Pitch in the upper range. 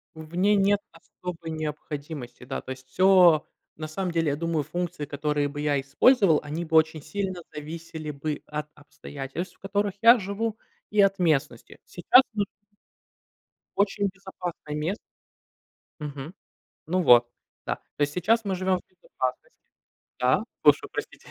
No: medium, 165 Hz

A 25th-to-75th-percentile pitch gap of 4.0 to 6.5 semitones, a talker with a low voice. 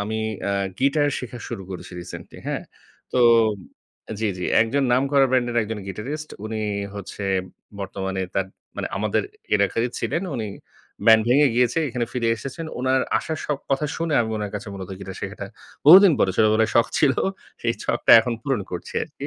Yes: average, 4.8 semitones; low, 115 Hz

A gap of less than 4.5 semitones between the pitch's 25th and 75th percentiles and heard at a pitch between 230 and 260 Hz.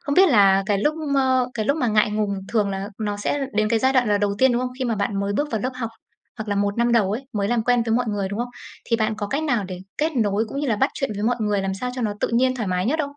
No: average, 3.8 semitones; high, 220 Hz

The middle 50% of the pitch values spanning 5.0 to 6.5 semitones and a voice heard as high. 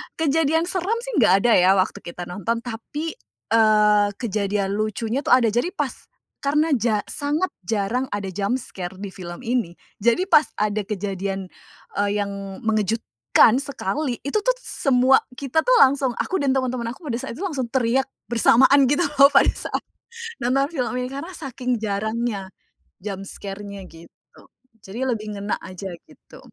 Yes: average, 5.3 semitones; high, 230 Hz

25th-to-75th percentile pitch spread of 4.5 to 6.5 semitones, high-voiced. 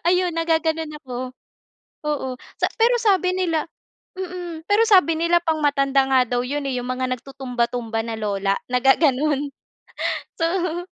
Yes: average, 5.3 semitones; very high, 300 Hz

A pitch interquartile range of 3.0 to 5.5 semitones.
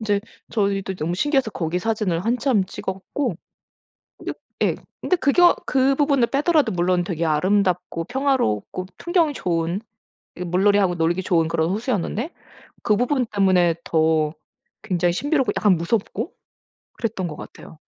No: wide, 6.2 semitones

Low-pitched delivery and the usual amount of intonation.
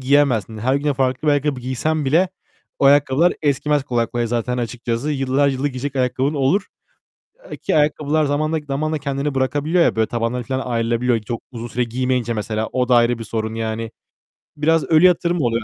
Yes: low, 130 Hz; average, 3.6 semitones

